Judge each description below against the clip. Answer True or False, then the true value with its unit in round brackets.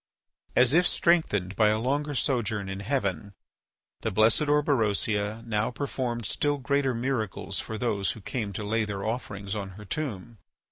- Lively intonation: False (4.5 semitones)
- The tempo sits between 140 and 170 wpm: True (155 wpm)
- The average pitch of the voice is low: True (110 Hz)